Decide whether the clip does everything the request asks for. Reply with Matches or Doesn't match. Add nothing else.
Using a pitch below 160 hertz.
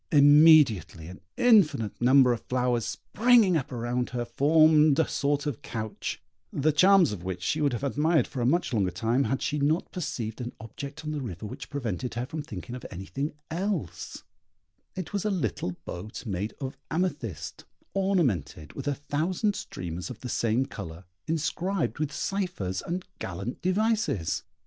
Matches